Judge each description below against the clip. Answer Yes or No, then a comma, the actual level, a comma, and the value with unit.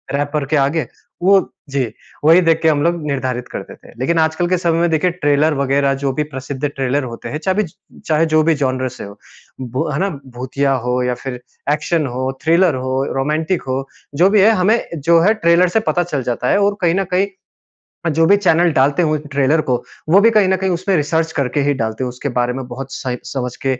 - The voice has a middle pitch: Yes, medium, 150 Hz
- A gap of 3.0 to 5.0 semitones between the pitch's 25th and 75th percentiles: Yes, average, 4.3 semitones